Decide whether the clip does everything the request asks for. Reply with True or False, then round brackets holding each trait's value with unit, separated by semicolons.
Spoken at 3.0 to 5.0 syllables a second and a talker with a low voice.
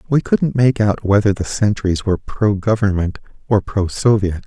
True (4.8 syllables/s; 105 Hz)